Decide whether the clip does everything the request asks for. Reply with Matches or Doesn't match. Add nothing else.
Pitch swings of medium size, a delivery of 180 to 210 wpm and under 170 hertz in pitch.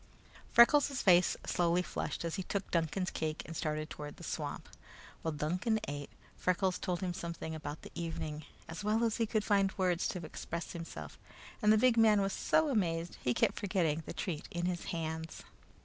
Doesn't match